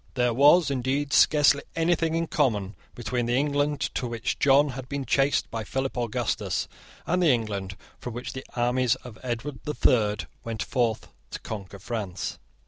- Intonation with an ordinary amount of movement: Yes, average, 3.9 semitones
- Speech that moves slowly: No, average, 165 wpm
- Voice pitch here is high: No, low, 125 Hz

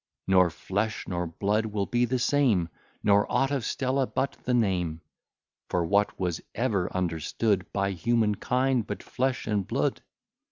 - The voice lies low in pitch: Yes, low, 105 Hz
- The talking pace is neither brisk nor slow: Yes, average, 155 wpm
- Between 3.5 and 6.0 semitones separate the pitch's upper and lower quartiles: Yes, average, 5.0 semitones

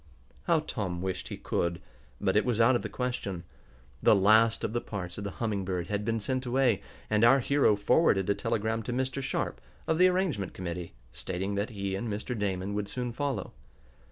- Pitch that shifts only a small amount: No, average, 4.3 semitones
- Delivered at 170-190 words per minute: No, average, 200 wpm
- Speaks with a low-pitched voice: Yes, low, 105 Hz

